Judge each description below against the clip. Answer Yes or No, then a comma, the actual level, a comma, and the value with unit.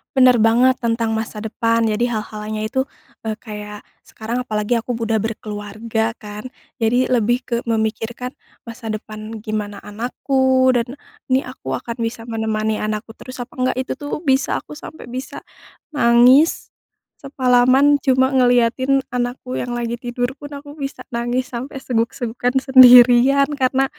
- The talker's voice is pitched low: No, high, 240 Hz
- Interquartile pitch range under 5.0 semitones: Yes, average, 2.7 semitones